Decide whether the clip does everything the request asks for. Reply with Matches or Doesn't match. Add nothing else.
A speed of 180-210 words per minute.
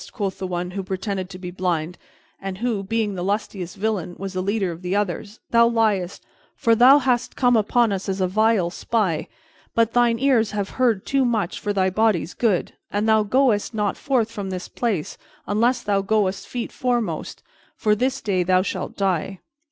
Matches